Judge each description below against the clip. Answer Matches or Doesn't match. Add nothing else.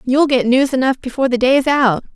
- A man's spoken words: Doesn't match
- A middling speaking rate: Doesn't match